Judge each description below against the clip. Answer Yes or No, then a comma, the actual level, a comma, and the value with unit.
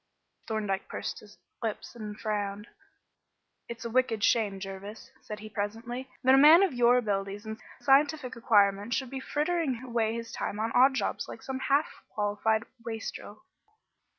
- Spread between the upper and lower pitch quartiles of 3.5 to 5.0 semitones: Yes, average, 3.8 semitones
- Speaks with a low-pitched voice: No, high, 225 Hz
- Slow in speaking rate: No, average, 160 wpm